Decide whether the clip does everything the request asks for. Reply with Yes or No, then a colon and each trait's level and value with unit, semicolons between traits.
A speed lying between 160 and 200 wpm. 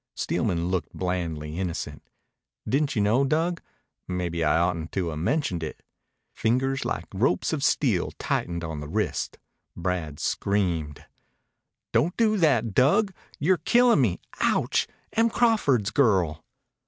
No: slow, 135 wpm